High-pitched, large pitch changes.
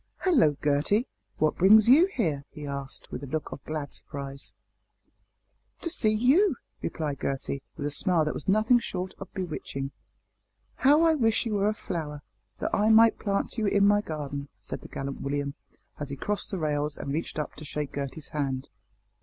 No: medium, 155 Hz; wide, 7.1 semitones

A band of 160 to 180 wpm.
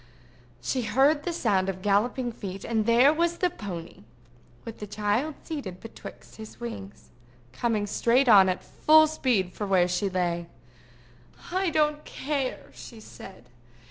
No: average, 145 wpm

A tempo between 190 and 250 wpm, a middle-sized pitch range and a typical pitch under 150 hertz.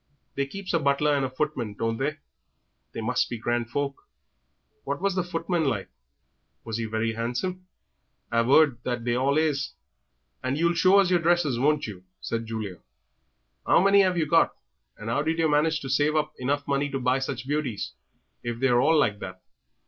Yes: average, 195 wpm; average, 5.0 semitones; medium, 140 Hz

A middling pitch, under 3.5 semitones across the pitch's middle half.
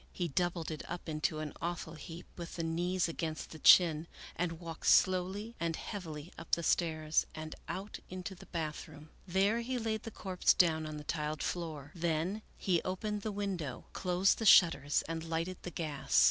Yes: medium, 170 Hz; average, 2.7 semitones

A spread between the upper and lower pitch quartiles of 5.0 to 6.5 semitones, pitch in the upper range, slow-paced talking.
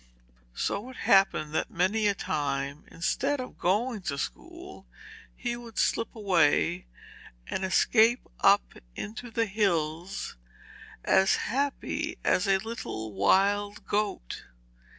Yes: wide, 5.5 semitones; high, 200 Hz; slow, 115 wpm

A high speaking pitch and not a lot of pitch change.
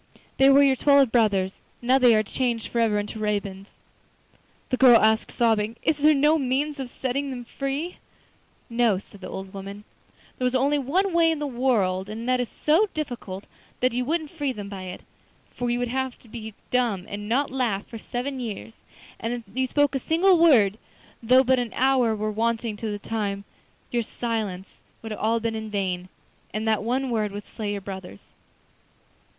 No: high, 235 Hz; average, 4.2 semitones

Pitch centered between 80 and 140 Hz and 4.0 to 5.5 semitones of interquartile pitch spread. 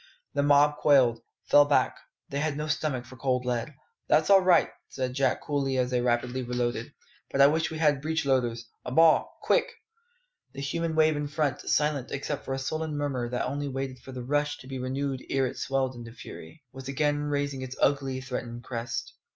No: low, 135 Hz; narrow, 2.5 semitones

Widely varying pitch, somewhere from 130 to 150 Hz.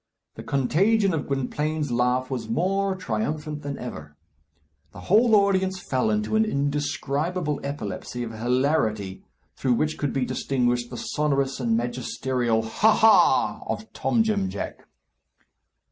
Yes: wide, 6.6 semitones; medium, 140 Hz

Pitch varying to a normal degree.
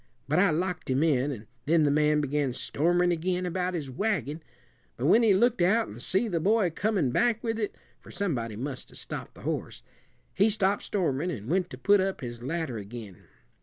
No: wide, 6.2 semitones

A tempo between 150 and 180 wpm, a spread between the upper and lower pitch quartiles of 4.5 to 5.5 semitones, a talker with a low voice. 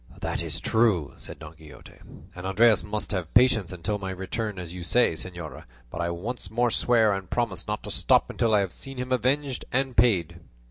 No: average, 200 wpm; average, 5.1 semitones; low, 105 Hz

